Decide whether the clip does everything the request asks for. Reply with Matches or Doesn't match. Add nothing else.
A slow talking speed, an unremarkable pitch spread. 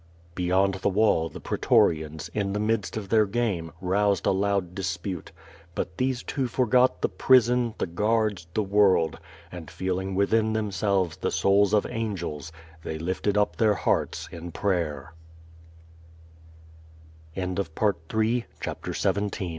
Matches